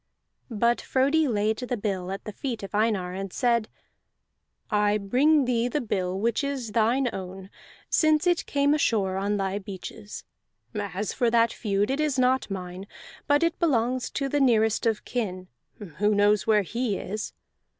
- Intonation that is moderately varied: Yes, average, 4.4 semitones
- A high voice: Yes, high, 220 Hz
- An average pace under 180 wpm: Yes, average, 165 wpm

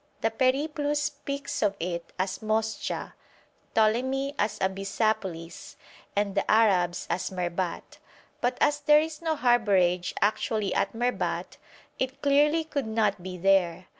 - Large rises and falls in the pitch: Yes, wide, 6.4 semitones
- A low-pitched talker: No, high, 220 Hz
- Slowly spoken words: Yes, slow, 130 wpm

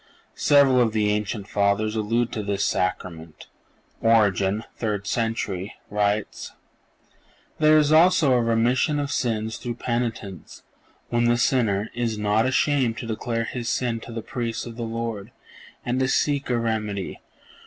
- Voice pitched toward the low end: Yes, low, 115 Hz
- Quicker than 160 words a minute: No, average, 150 wpm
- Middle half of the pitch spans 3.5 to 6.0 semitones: No, average, 2.7 semitones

